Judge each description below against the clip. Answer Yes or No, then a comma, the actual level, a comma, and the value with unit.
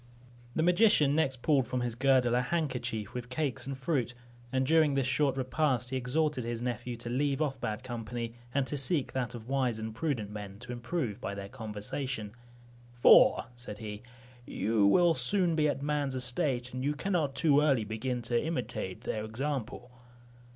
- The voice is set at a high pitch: No, low, 130 Hz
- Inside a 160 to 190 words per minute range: Yes, average, 180 wpm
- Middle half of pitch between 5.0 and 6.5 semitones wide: No, average, 3.5 semitones